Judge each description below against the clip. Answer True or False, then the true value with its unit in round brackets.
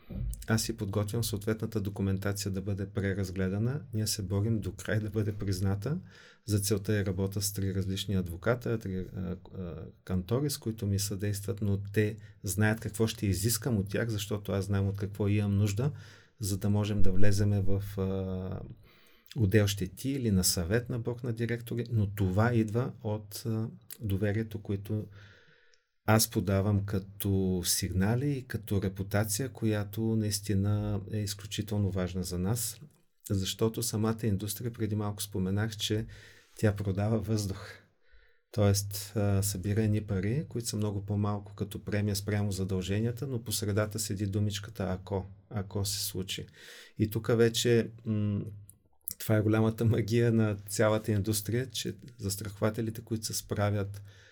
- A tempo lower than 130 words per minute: False (145 wpm)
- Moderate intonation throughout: False (2.0 semitones)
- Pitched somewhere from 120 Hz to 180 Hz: False (105 Hz)